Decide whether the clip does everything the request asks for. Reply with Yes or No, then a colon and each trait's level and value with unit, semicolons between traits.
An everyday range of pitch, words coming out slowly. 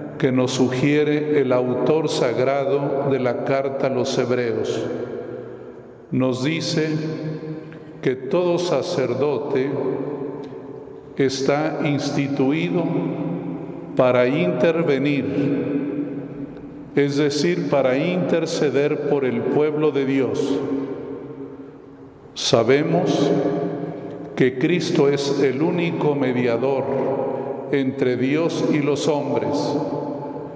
No: narrow, 1.7 semitones; slow, 80 wpm